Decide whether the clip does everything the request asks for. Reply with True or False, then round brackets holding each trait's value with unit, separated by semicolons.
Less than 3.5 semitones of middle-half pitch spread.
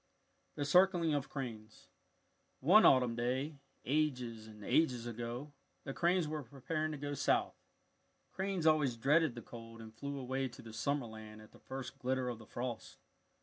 False (4.4 semitones)